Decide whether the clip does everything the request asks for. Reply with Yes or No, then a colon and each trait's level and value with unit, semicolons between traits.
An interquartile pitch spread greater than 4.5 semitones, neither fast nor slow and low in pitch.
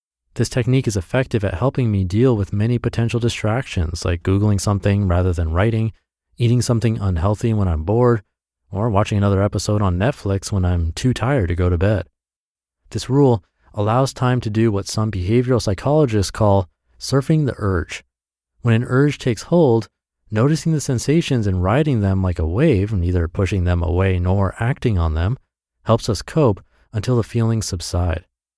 Yes: average, 4.9 semitones; average, 170 wpm; low, 105 Hz